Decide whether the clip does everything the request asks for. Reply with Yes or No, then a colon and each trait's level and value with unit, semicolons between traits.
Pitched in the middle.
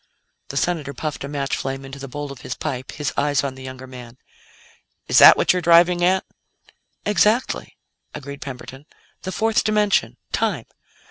Yes: medium, 145 Hz